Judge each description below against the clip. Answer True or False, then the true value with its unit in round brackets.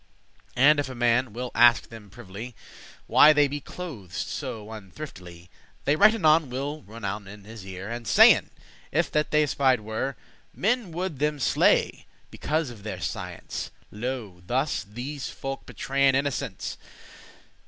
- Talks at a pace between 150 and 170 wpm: True (155 wpm)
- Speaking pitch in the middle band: False (125 Hz)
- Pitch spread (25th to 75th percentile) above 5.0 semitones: True (5.4 semitones)